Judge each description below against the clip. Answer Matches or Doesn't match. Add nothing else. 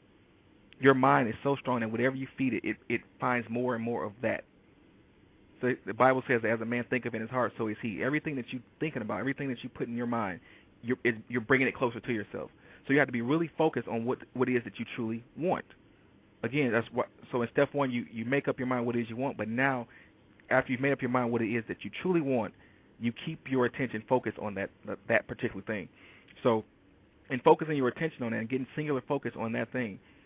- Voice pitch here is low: Matches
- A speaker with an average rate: Doesn't match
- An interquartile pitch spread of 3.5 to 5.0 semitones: Doesn't match